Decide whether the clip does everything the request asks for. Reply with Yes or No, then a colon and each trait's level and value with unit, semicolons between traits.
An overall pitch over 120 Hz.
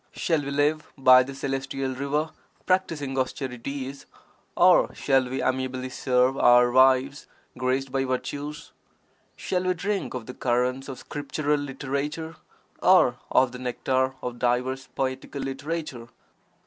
Yes: low, 135 Hz